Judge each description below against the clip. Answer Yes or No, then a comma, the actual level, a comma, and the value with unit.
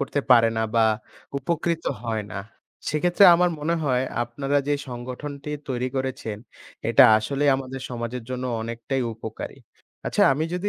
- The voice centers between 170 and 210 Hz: No, low, 130 Hz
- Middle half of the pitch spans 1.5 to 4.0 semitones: Yes, average, 3.5 semitones